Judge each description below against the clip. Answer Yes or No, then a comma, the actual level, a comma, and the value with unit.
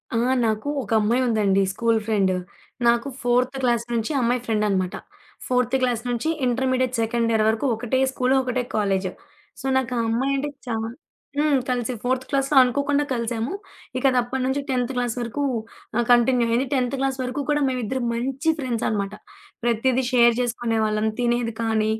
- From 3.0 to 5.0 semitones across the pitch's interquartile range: No, narrow, 2.4 semitones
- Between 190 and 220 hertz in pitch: No, high, 245 Hz